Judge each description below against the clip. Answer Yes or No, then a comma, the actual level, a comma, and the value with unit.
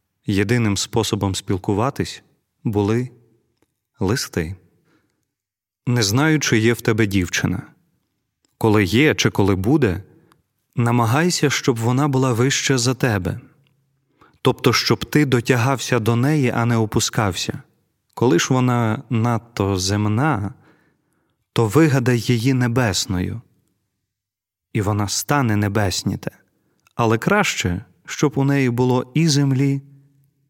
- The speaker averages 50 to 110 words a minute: Yes, slow, 105 wpm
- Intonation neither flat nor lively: Yes, average, 4.7 semitones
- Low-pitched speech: Yes, low, 120 Hz